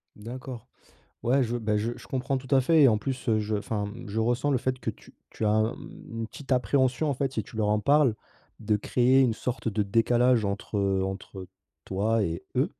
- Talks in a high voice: No, low, 115 Hz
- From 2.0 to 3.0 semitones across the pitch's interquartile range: No, average, 3.5 semitones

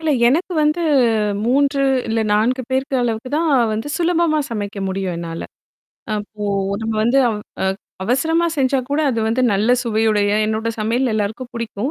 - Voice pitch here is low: No, high, 235 Hz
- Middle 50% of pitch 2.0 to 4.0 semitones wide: No, average, 4.4 semitones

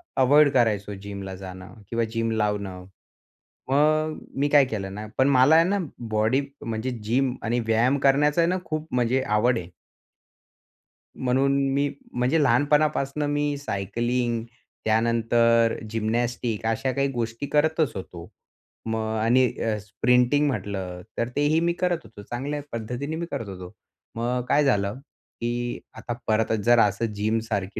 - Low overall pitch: Yes, low, 120 Hz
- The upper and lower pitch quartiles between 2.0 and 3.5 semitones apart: No, average, 4.3 semitones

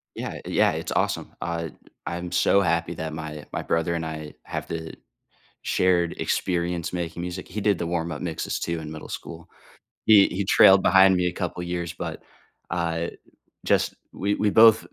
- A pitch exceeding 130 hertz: No, very low, 85 Hz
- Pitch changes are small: Yes, narrow, 1.9 semitones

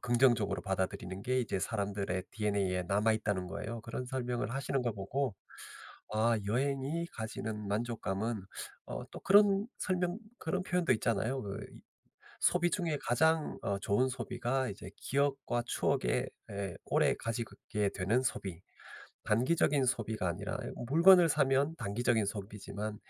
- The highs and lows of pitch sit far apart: No, average, 5.0 semitones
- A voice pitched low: Yes, low, 115 Hz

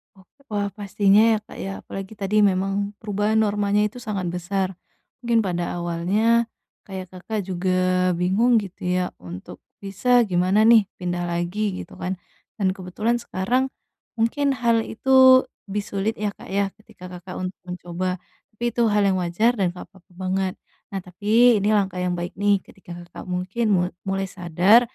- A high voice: Yes, high, 195 Hz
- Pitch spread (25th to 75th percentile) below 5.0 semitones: Yes, average, 2.8 semitones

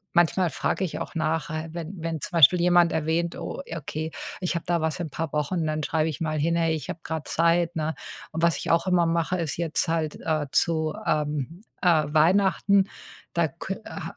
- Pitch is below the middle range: No, medium, 165 Hz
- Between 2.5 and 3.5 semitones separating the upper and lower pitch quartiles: No, narrow, 1.7 semitones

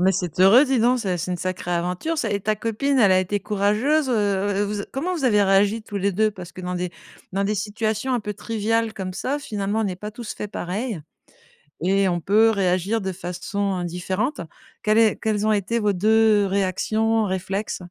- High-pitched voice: Yes, high, 205 Hz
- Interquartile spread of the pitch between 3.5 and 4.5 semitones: No, average, 3.0 semitones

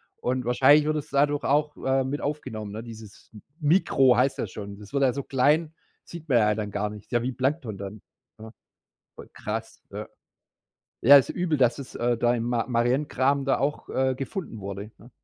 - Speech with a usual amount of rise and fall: Yes, average, 4.1 semitones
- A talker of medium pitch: No, low, 130 Hz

